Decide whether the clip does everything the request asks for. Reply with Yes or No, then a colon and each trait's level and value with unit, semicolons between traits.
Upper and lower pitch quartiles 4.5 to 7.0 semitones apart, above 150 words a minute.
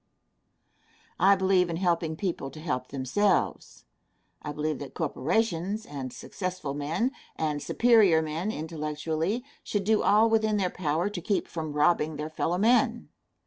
No: average, 5.1 semitones; average, 145 wpm